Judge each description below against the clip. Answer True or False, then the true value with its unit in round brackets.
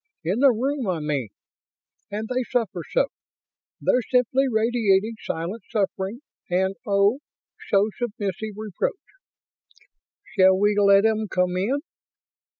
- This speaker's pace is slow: True (120 wpm)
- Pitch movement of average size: True (3.9 semitones)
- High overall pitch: True (210 Hz)